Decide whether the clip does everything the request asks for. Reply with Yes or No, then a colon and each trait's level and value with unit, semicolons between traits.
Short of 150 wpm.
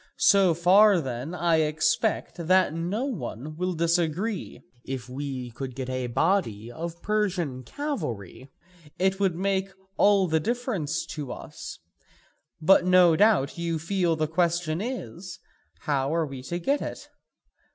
Yes: average, 140 wpm